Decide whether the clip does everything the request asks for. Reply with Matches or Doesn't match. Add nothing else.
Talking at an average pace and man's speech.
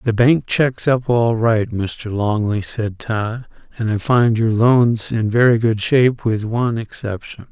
Matches